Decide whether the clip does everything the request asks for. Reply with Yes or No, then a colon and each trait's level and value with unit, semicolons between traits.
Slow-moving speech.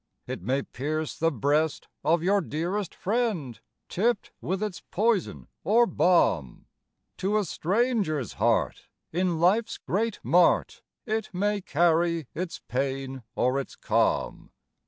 Yes: slow, 125 wpm